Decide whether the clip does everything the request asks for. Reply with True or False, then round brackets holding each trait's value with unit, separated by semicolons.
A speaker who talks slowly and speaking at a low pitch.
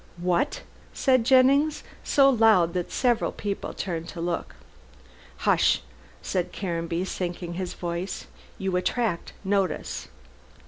False (110 wpm; 190 Hz)